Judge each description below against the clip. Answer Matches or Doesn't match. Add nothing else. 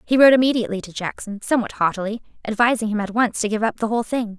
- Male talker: Doesn't match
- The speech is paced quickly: Matches